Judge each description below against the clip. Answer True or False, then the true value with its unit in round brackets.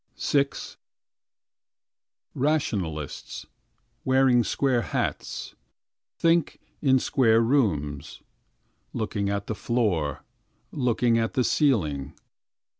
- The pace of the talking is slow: True (80 wpm)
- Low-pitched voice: True (115 Hz)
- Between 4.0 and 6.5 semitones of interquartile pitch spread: True (5.2 semitones)